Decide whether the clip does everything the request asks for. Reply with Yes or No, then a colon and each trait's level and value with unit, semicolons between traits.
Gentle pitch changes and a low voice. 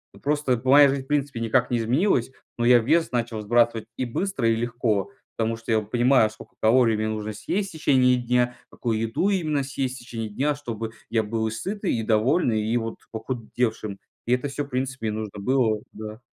No: average, 3.2 semitones; low, 120 Hz